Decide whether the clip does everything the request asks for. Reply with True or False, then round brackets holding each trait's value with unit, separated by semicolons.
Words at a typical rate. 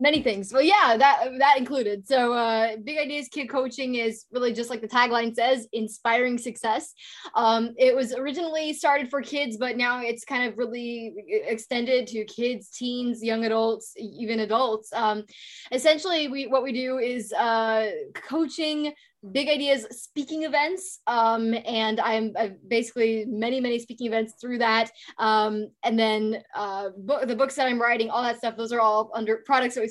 True (175 wpm)